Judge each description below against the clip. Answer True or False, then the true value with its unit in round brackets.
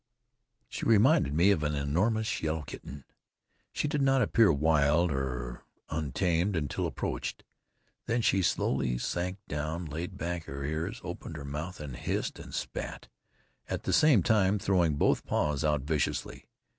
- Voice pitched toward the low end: True (80 Hz)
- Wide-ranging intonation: False (5.0 semitones)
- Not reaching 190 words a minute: True (150 wpm)